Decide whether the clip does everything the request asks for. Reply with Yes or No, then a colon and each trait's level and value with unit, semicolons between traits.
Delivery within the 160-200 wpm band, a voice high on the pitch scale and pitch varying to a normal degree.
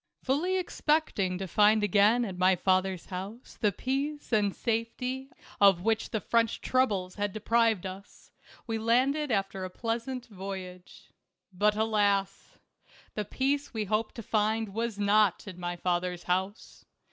No: average, 145 wpm; high, 210 Hz; average, 3.5 semitones